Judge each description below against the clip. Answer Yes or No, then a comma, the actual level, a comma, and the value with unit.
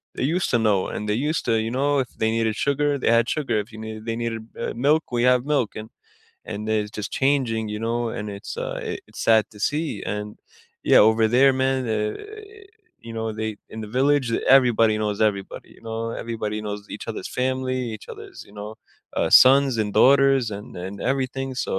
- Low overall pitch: Yes, low, 115 Hz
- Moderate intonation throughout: Yes, average, 3.7 semitones